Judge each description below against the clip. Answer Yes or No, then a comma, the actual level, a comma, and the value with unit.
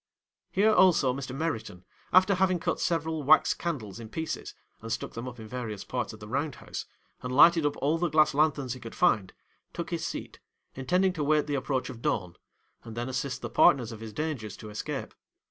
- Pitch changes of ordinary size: No, wide, 5.8 semitones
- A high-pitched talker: No, low, 135 Hz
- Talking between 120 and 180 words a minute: No, fast, 205 wpm